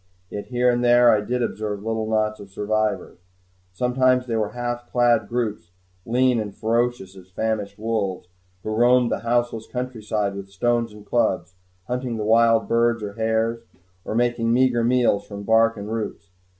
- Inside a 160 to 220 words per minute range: Yes, average, 165 wpm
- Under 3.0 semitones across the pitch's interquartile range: Yes, narrow, 2.4 semitones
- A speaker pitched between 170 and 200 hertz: No, low, 115 Hz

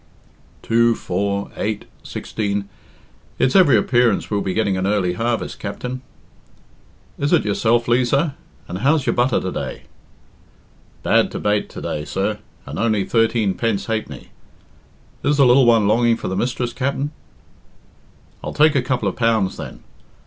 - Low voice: Yes, low, 115 Hz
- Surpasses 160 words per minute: No, average, 150 wpm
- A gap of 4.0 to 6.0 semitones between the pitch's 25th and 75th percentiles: No, average, 3.6 semitones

